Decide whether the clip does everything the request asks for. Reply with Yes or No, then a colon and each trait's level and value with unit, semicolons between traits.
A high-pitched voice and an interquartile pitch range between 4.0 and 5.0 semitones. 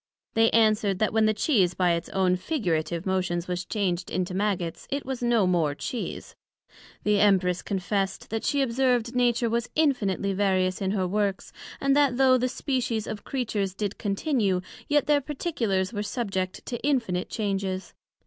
Yes: high, 205 Hz; average, 4.6 semitones